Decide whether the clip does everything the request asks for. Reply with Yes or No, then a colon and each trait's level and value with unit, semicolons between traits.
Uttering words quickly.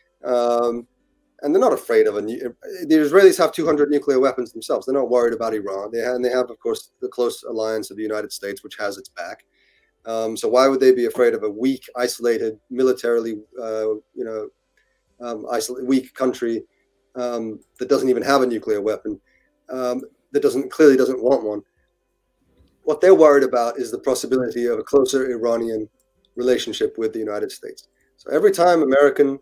Yes: fast, 190 wpm